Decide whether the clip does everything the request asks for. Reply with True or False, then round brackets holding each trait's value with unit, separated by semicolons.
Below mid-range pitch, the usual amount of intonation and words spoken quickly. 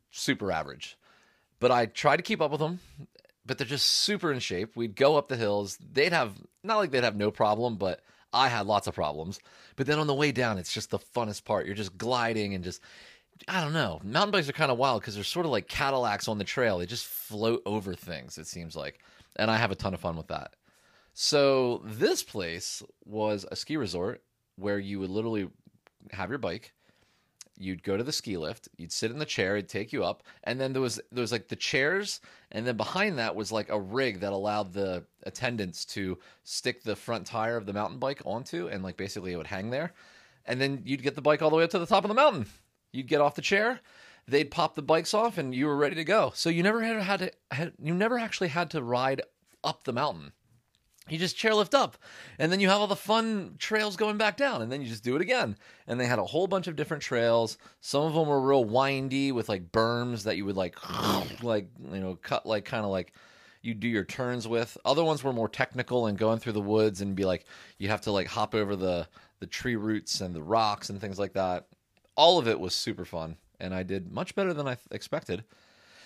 False (120 Hz; 6.6 semitones; 240 wpm)